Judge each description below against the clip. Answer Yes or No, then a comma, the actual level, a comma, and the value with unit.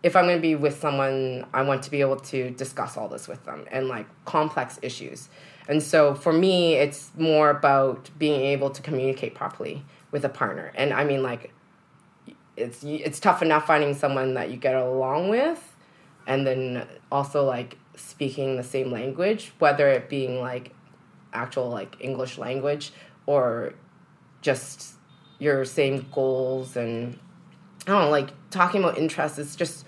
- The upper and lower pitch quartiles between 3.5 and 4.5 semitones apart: No, average, 3.0 semitones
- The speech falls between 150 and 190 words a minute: Yes, average, 165 wpm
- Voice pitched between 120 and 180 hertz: Yes, medium, 140 Hz